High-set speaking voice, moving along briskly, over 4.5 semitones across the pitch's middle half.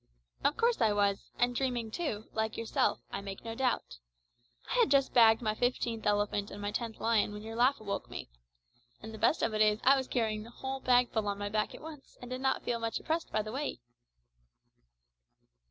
No: high, 225 Hz; fast, 215 wpm; average, 3.3 semitones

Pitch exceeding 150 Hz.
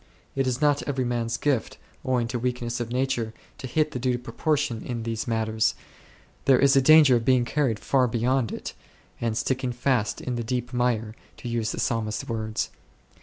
No: low, 120 Hz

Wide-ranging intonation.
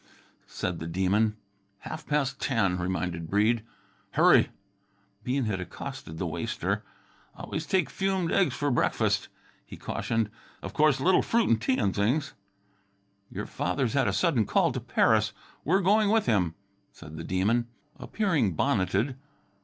Yes: wide, 8.6 semitones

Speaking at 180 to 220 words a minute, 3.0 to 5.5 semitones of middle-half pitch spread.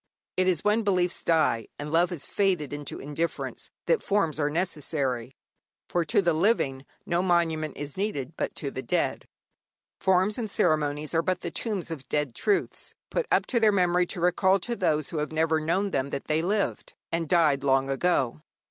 Yes: average, 185 wpm; average, 4.2 semitones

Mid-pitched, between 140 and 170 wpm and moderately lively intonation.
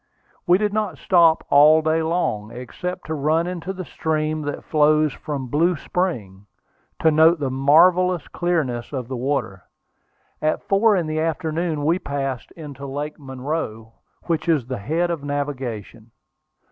Yes: medium, 155 Hz; average, 150 wpm; average, 3.9 semitones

